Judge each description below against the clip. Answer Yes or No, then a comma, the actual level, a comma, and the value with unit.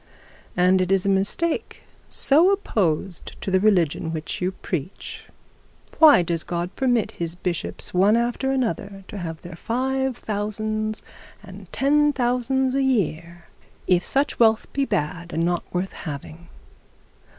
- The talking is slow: No, average, 145 wpm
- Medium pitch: No, high, 200 Hz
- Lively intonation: Yes, wide, 6.4 semitones